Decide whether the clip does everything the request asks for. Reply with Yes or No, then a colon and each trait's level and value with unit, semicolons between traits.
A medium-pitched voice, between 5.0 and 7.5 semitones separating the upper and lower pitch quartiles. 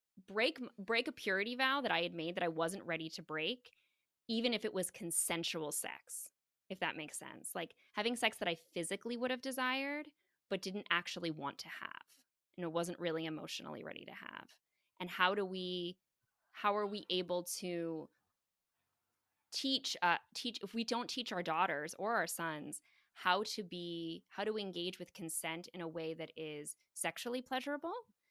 Yes: medium, 180 Hz; wide, 5.5 semitones